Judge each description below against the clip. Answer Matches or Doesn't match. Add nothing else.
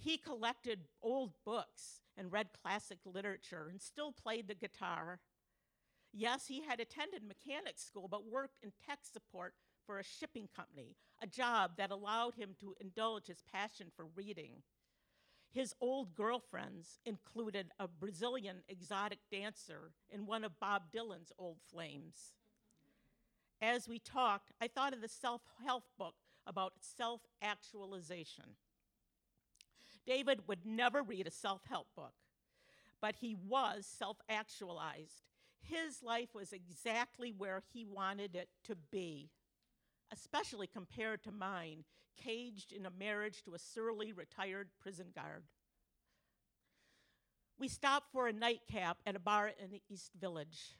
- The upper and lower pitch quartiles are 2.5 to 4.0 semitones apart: Matches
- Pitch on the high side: Matches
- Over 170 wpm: Doesn't match